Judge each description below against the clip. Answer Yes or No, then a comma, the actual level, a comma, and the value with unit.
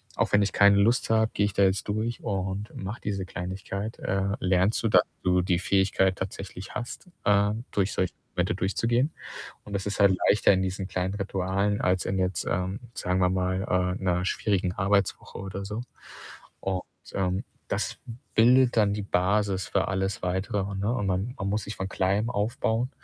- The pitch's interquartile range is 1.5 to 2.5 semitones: Yes, narrow, 1.8 semitones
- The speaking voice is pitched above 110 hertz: No, low, 100 Hz